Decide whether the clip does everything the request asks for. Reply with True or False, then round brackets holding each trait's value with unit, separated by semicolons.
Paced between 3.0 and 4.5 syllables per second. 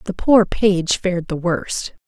True (3.9 syllables/s)